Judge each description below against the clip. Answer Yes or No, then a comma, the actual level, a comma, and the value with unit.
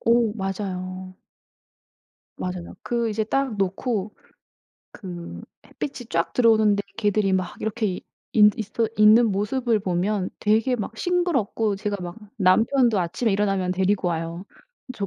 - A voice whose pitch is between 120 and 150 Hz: No, high, 210 Hz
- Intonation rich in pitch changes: No, average, 3.4 semitones